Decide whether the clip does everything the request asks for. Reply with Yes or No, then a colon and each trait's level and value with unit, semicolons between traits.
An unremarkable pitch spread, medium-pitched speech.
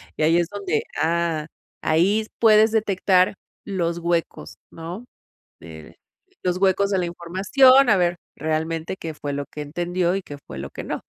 Yes: average, 3.5 semitones; medium, 175 Hz